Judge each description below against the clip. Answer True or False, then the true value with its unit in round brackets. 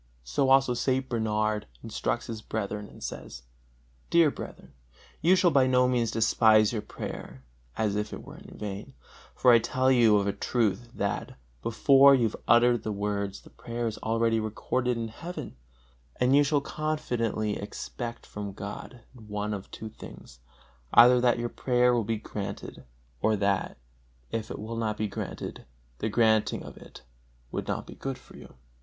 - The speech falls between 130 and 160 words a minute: False (170 wpm)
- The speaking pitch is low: True (115 Hz)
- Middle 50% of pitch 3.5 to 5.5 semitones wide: False (3.0 semitones)